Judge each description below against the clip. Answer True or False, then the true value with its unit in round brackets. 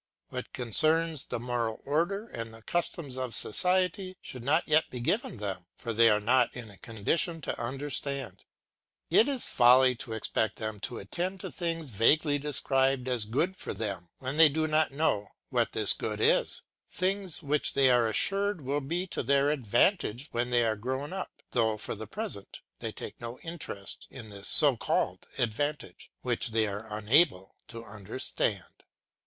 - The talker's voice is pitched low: True (130 Hz)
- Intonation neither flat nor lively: False (6.0 semitones)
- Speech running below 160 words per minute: False (175 wpm)